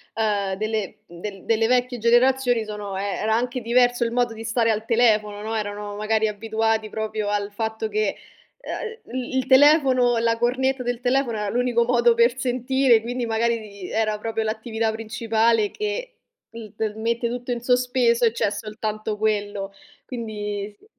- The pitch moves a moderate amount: No, narrow, 2.3 semitones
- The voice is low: No, high, 225 Hz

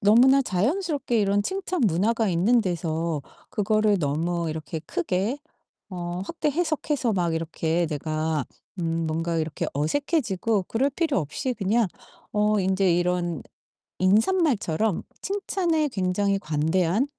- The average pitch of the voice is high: Yes, high, 195 Hz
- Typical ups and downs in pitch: No, wide, 6.6 semitones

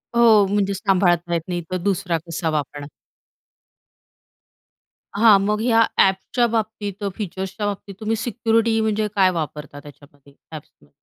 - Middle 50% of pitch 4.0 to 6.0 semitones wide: Yes, average, 4.4 semitones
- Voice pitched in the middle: No, high, 195 Hz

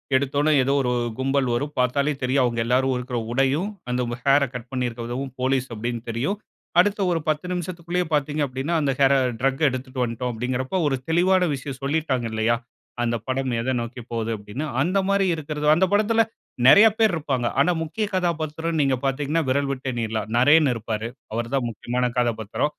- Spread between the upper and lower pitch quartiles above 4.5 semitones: No, average, 4.0 semitones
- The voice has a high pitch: No, low, 135 Hz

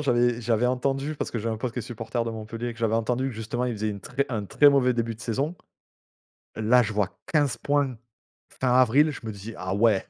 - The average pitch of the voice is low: Yes, low, 120 Hz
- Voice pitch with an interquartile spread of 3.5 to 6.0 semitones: No, average, 2.7 semitones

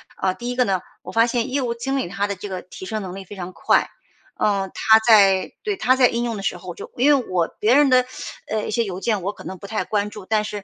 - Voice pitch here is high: Yes, high, 210 Hz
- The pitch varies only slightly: No, average, 3.7 semitones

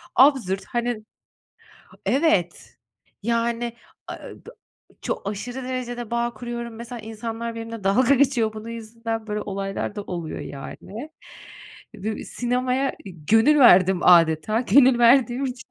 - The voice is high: Yes, high, 230 Hz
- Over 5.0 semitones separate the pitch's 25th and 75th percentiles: No, average, 2.9 semitones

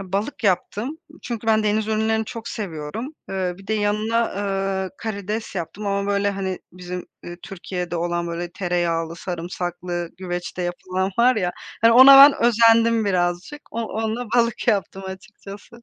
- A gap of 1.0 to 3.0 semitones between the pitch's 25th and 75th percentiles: No, average, 3.7 semitones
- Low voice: No, high, 200 Hz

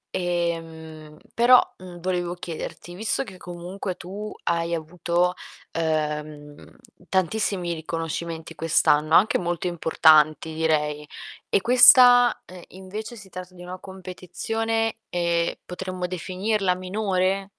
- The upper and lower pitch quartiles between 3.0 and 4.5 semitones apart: No, narrow, 2.6 semitones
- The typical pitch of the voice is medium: Yes, medium, 180 Hz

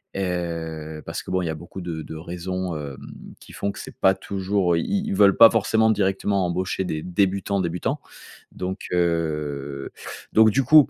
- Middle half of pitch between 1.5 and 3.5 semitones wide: Yes, average, 3.2 semitones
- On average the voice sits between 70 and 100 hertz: Yes, very low, 90 Hz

